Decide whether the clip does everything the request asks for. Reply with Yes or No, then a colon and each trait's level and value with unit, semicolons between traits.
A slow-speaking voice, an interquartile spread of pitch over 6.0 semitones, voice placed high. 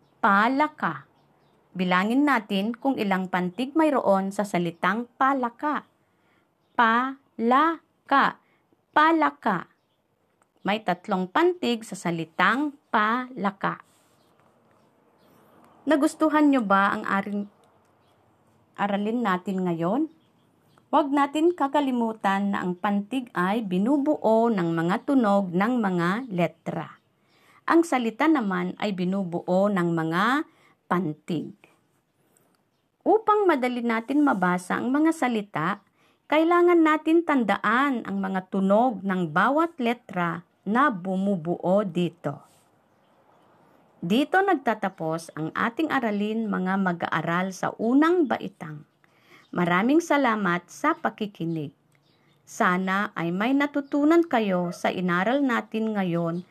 Yes: slow, 95 wpm; wide, 7.2 semitones; high, 205 Hz